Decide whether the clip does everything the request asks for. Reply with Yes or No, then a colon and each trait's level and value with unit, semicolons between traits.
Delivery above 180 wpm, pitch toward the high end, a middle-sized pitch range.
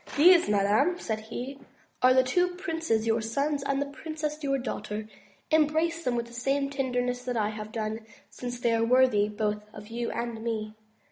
Yes: average, 190 wpm; high, 245 Hz; average, 4.4 semitones